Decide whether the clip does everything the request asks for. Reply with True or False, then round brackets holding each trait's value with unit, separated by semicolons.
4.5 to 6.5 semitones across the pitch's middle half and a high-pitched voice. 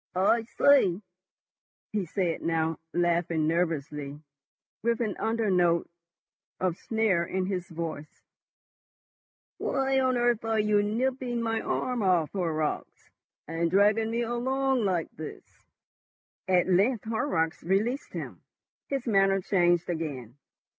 True (5.3 semitones; 195 Hz)